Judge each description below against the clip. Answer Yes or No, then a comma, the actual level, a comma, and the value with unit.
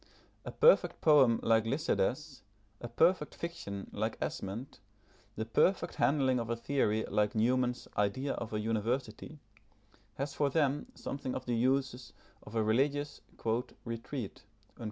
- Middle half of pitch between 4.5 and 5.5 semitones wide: No, average, 4.1 semitones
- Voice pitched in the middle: No, low, 125 Hz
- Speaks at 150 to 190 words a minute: No, slow, 135 wpm